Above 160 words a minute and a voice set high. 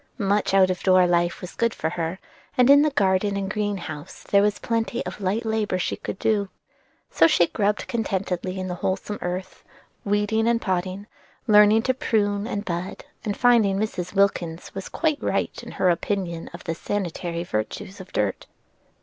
Yes: average, 175 wpm; high, 195 Hz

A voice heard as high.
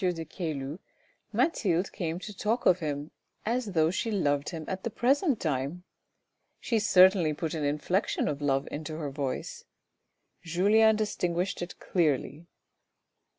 No: medium, 170 Hz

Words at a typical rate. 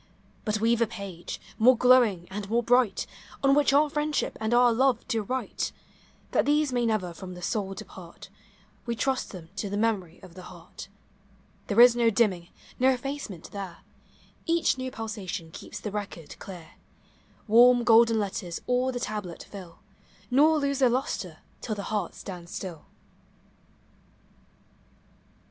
Yes: average, 155 wpm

